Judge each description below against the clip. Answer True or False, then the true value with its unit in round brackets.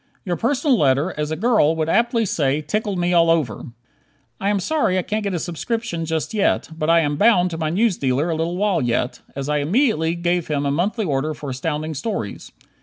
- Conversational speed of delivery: False (210 wpm)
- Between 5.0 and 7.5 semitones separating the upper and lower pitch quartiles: True (5.3 semitones)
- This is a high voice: False (165 Hz)